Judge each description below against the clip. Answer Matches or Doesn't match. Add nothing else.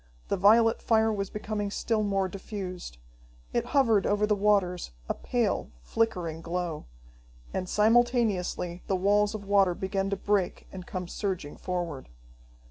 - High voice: Matches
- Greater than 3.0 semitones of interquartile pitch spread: Doesn't match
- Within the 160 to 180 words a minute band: Doesn't match